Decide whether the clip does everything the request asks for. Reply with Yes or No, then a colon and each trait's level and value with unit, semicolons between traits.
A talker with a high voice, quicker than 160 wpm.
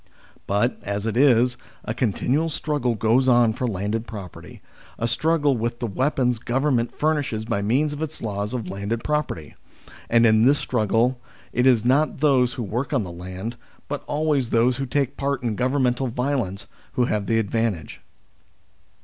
No: low, 120 Hz; average, 170 wpm